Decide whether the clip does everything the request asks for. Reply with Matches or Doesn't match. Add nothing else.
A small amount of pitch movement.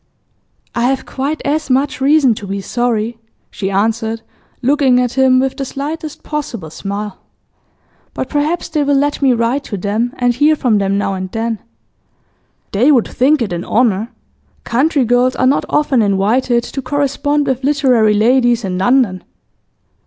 Doesn't match